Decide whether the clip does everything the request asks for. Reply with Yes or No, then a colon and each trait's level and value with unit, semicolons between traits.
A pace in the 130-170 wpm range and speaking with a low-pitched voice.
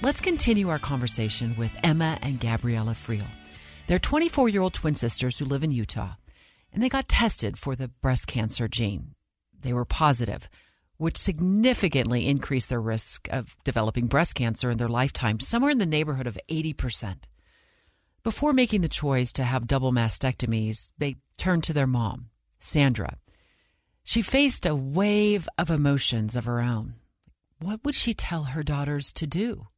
Yes: average, 160 wpm; low, 130 Hz